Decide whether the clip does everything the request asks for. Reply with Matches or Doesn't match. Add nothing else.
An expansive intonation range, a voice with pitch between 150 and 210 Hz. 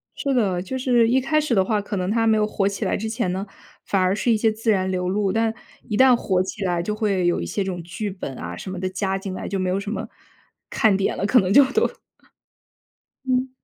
Doesn't match